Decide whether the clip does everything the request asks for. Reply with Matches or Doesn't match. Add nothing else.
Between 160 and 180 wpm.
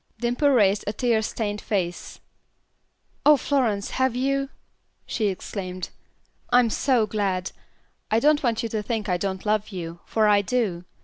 Doesn't match